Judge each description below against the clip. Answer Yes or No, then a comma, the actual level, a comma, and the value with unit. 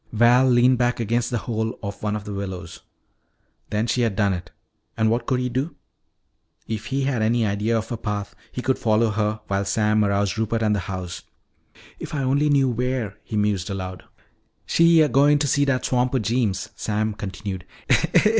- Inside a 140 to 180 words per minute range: No, average, 190 wpm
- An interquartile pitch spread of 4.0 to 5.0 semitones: No, average, 3.5 semitones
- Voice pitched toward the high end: No, low, 110 Hz